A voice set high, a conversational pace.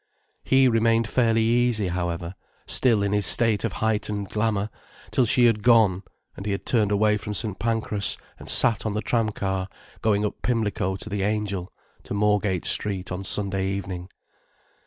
No: low, 105 Hz; average, 170 wpm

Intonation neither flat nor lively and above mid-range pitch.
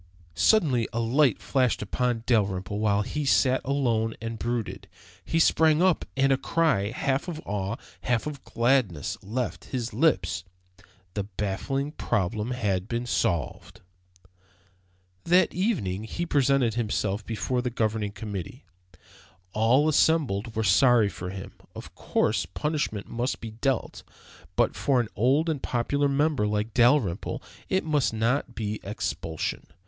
No: average, 4.7 semitones; low, 120 Hz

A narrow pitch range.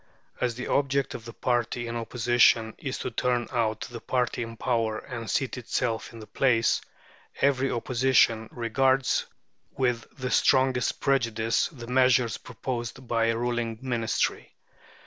Yes: narrow, 2.0 semitones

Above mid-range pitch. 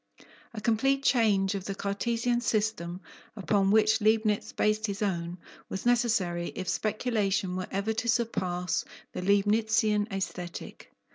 Yes: high, 210 Hz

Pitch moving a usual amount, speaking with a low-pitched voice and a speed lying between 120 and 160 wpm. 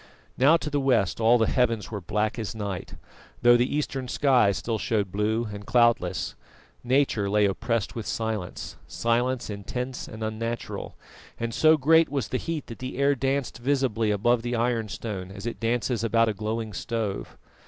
No: average, 3.0 semitones; low, 115 Hz; average, 170 wpm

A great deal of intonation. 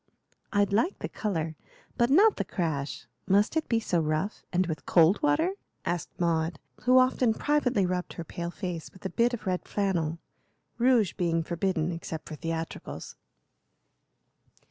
Yes: wide, 5.9 semitones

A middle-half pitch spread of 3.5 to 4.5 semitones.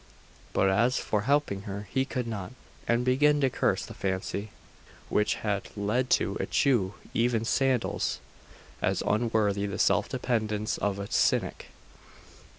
Yes: average, 3.8 semitones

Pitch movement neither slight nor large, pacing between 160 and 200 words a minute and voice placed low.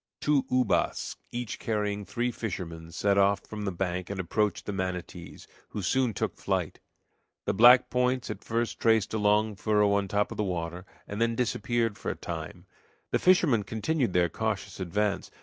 Yes: average, 3.4 semitones; average, 180 wpm; low, 105 Hz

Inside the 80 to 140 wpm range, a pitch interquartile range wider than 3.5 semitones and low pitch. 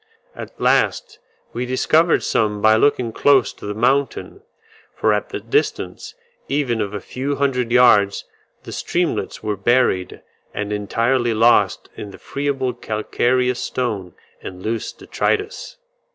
Yes: slow, 135 wpm; average, 3.9 semitones; low, 120 Hz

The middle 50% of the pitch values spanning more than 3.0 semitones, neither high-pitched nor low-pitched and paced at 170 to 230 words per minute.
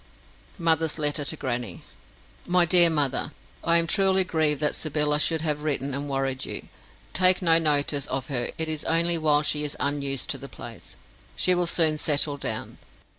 No: narrow, 2.6 semitones; medium, 150 Hz; average, 175 wpm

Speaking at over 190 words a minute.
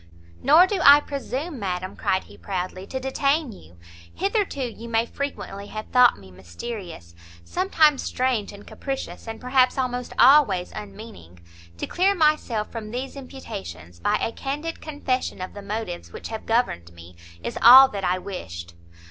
No: average, 155 wpm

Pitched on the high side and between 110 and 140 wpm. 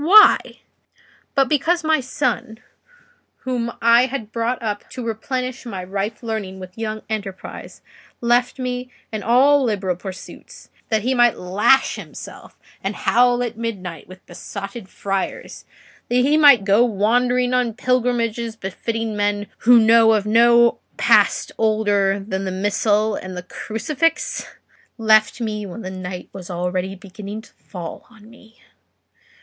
Yes: high, 220 Hz; slow, 135 wpm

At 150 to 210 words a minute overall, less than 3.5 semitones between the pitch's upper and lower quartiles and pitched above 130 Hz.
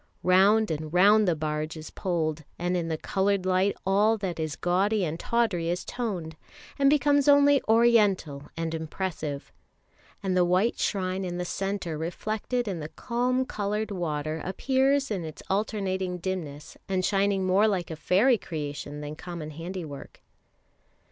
No: average, 155 wpm; average, 4.5 semitones; medium, 185 Hz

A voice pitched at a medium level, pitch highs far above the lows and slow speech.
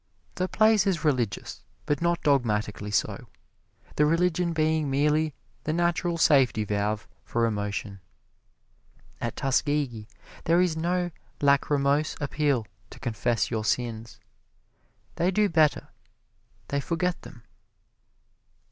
Yes: medium, 145 Hz; wide, 6.2 semitones; slow, 110 wpm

